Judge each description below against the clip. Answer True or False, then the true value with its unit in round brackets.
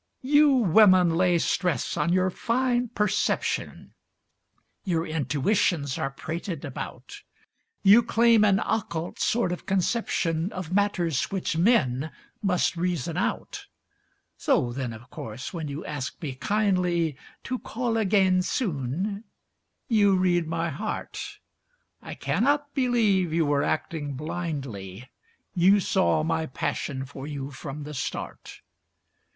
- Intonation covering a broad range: True (5.8 semitones)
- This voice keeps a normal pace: False (125 wpm)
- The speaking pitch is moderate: True (175 Hz)